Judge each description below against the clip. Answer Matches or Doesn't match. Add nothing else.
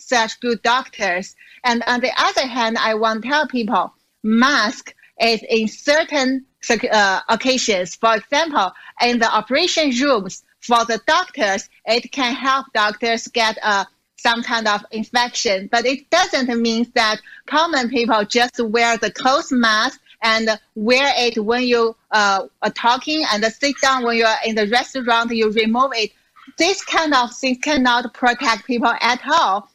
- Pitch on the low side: Doesn't match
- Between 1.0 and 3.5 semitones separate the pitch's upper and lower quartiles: Matches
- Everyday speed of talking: Matches